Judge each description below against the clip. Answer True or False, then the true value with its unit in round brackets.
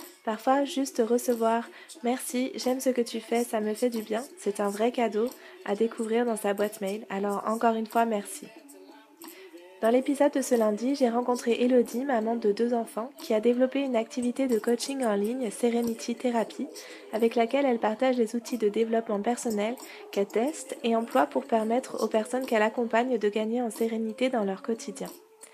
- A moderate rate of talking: True (185 wpm)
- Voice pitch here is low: False (235 Hz)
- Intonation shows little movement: True (2.3 semitones)